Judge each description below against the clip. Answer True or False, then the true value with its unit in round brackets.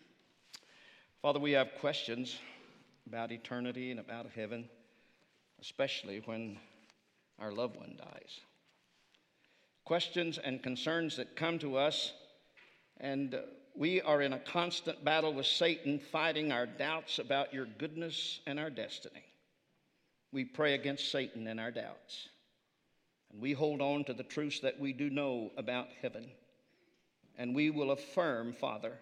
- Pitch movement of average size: True (3.9 semitones)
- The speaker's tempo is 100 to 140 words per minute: True (135 wpm)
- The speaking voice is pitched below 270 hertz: True (140 Hz)